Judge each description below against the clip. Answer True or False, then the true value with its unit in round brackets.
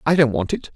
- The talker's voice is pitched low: True (130 Hz)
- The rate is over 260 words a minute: True (320 wpm)